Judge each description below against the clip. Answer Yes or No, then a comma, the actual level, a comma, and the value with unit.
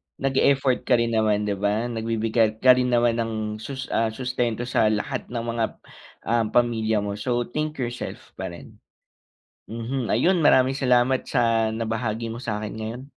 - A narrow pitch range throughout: Yes, narrow, 2.3 semitones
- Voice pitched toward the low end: Yes, low, 115 Hz